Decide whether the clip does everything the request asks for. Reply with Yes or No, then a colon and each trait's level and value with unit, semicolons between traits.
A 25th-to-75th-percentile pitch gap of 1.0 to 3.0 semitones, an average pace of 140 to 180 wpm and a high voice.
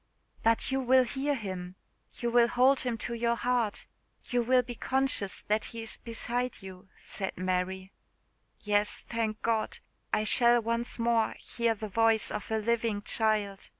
Yes: narrow, 2.5 semitones; average, 160 wpm; high, 230 Hz